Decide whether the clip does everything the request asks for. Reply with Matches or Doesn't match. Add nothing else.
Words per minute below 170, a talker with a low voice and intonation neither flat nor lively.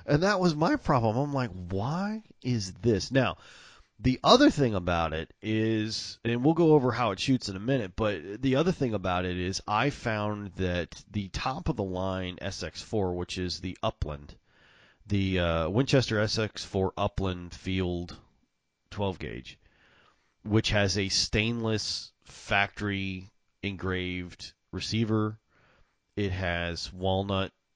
Matches